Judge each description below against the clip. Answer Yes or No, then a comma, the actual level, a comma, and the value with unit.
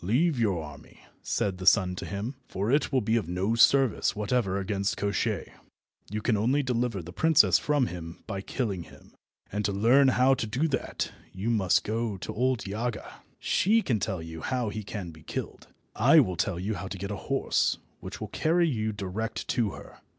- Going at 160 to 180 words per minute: No, fast, 205 wpm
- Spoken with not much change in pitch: No, average, 4.5 semitones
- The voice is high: No, low, 105 Hz